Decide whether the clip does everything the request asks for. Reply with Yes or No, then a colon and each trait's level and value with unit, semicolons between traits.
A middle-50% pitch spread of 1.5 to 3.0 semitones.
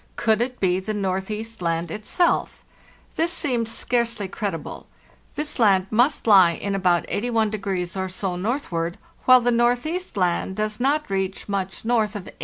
No: average, 4.3 semitones